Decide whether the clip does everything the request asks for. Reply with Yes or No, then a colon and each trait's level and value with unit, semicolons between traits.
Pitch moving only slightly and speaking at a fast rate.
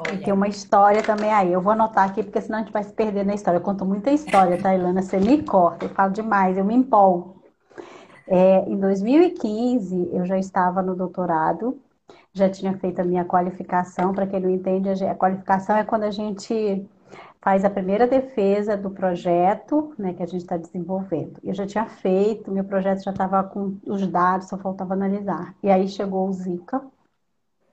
Yes: narrow, 2.0 semitones; fast, 195 wpm